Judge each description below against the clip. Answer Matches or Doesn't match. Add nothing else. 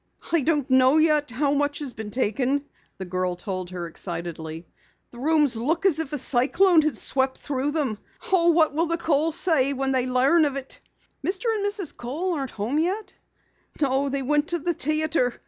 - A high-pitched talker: Matches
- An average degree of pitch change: Matches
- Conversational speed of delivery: Matches